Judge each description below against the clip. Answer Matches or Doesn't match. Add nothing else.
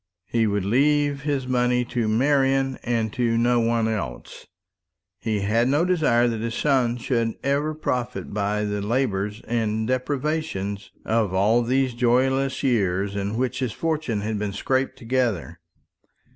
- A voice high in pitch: Doesn't match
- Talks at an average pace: Matches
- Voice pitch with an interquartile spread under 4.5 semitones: Matches